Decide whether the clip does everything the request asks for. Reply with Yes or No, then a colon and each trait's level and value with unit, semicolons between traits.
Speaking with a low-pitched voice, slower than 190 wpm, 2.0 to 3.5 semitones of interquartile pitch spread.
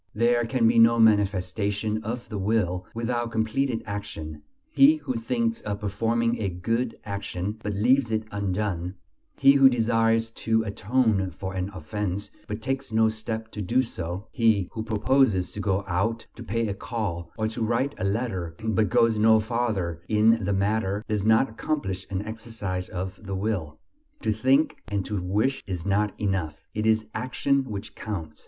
Yes: low, 110 Hz; average, 170 wpm; average, 2.8 semitones